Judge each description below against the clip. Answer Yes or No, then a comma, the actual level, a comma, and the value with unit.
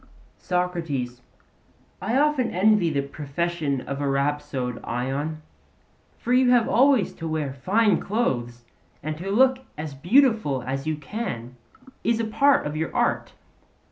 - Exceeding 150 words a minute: No, average, 140 wpm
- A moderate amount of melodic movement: No, wide, 8.1 semitones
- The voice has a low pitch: No, medium, 160 Hz